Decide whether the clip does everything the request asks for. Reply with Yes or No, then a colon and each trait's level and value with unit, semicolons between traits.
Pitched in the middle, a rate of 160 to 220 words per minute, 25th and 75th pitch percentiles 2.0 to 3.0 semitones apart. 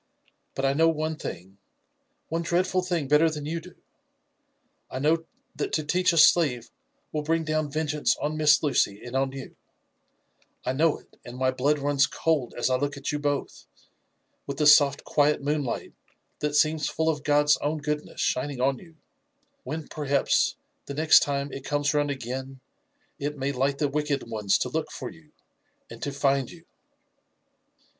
Yes: medium, 145 Hz; average, 180 wpm; narrow, 2.4 semitones